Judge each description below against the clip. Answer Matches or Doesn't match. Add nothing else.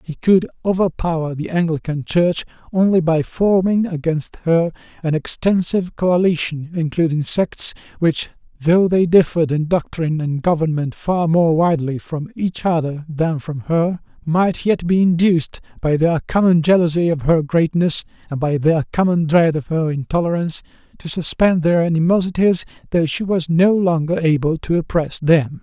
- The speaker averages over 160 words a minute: Doesn't match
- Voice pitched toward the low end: Doesn't match